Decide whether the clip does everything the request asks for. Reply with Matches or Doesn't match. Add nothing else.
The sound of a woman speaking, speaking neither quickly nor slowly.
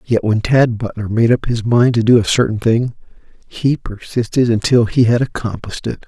Doesn't match